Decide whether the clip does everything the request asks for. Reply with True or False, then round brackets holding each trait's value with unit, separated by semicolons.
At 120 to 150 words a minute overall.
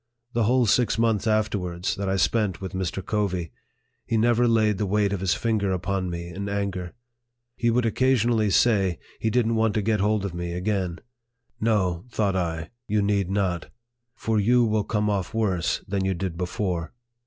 False (190 wpm)